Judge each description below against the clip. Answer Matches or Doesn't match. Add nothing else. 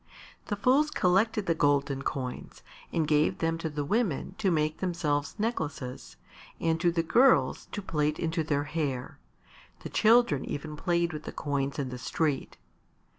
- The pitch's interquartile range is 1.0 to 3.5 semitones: Doesn't match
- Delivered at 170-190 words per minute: Doesn't match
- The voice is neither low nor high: Matches